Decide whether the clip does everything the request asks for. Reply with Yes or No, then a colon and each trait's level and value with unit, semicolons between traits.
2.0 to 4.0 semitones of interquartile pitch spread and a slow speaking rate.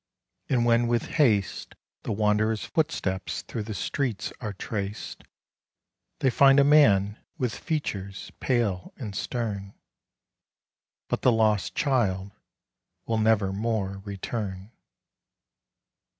Yes: average, 3.4 semitones; slow, 105 wpm